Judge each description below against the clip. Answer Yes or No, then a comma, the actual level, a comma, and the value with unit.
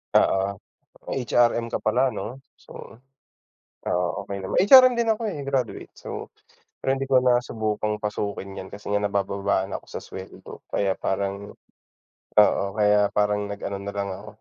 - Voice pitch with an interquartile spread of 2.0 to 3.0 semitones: No, average, 3.6 semitones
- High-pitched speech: No, low, 105 Hz